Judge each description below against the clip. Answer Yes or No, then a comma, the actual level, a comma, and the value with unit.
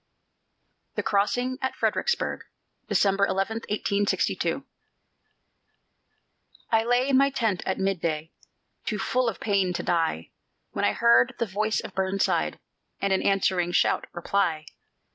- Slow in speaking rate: Yes, slow, 130 wpm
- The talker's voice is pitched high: Yes, high, 195 Hz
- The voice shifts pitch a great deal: No, average, 3.7 semitones